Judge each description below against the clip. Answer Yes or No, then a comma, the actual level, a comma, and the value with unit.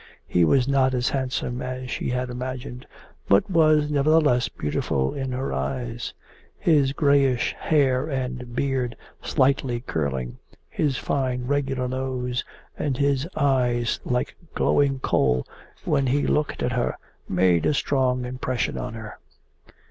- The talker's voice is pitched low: Yes, low, 130 Hz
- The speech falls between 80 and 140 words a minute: Yes, slow, 135 wpm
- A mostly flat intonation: Yes, narrow, 2.1 semitones